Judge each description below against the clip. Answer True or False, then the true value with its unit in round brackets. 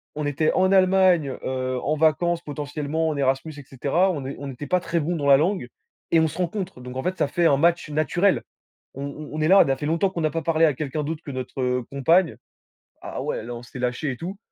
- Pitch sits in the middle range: True (155 Hz)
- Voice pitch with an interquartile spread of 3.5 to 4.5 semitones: True (3.9 semitones)